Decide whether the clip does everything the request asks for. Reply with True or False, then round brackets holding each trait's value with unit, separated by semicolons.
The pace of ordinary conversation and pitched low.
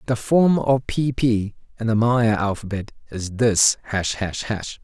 True (175 wpm; 110 Hz)